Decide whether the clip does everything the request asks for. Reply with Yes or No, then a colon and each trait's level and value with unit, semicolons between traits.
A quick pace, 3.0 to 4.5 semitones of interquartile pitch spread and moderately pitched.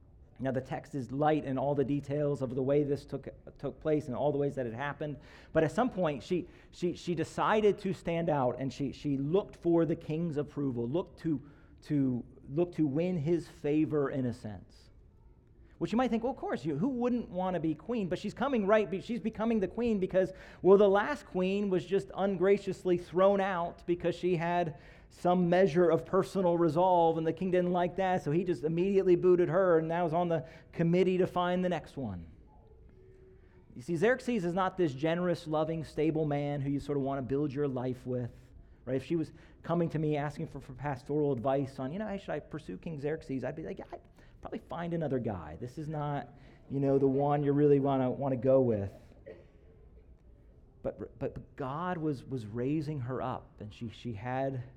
No: fast, 210 wpm; average, 4.9 semitones; medium, 155 Hz